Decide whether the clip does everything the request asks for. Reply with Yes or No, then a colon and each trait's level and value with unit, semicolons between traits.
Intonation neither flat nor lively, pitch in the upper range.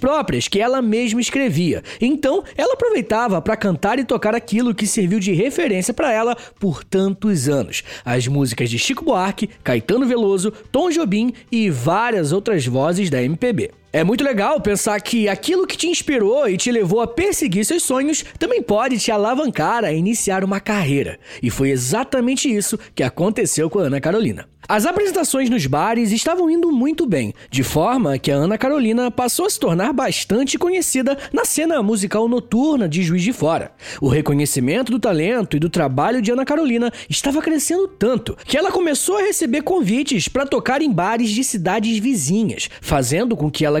No: wide, 6.3 semitones; high, 225 Hz